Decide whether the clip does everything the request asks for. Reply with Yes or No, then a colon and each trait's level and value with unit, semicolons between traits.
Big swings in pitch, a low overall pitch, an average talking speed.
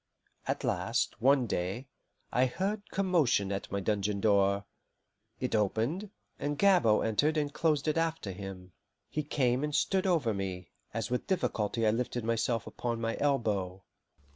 Yes: wide, 6.7 semitones; low, 120 Hz; average, 150 wpm